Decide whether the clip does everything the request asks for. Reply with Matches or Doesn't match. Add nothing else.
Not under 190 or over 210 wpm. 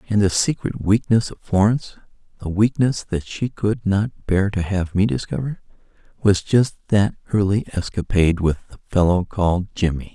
Doesn't match